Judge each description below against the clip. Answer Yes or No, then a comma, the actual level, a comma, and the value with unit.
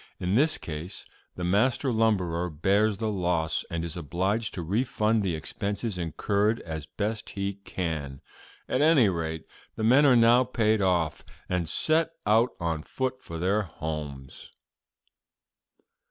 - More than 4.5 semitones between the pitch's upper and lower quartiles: Yes, average, 5.2 semitones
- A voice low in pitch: Yes, low, 100 Hz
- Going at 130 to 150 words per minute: Yes, average, 140 wpm